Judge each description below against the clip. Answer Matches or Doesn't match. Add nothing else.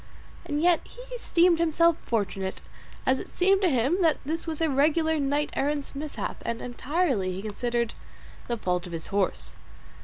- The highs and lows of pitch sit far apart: Matches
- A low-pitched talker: Doesn't match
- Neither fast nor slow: Matches